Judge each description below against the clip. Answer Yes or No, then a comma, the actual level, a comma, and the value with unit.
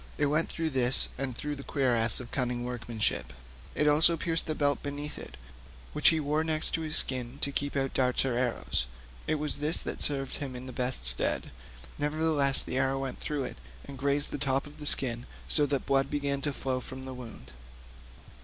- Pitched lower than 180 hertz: Yes, medium, 140 Hz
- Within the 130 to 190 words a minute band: No, average, 200 wpm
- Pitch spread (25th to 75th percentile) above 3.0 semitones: No, narrow, 2.6 semitones